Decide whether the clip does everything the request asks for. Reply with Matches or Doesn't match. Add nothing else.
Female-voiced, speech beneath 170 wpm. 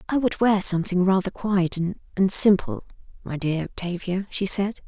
Matches